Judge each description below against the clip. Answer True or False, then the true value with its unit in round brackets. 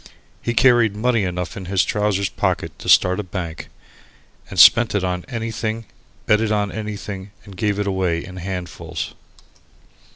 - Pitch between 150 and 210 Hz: False (100 Hz)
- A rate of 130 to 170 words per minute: True (160 wpm)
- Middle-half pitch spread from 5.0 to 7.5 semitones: False (2.9 semitones)